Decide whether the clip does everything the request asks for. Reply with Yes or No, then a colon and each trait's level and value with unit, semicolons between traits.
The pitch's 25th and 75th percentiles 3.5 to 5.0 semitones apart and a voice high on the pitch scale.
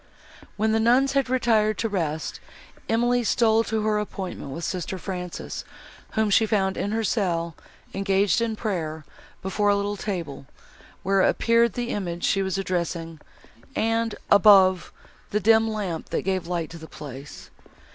Yes: average, 4.0 semitones; high, 200 Hz